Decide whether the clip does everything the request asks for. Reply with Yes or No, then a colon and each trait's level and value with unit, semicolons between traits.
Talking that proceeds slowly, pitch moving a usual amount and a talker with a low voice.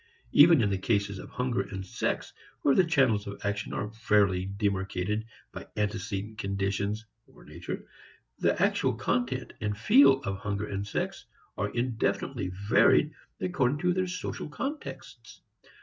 No: average, 145 wpm; average, 4.5 semitones; low, 105 Hz